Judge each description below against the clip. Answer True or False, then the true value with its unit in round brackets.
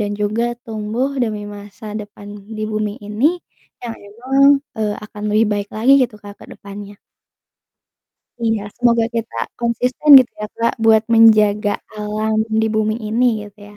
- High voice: True (215 Hz)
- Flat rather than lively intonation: True (1.8 semitones)